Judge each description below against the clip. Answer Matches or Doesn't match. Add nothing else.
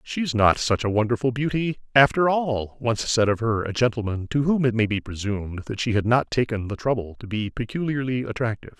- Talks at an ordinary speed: Doesn't match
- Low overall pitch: Matches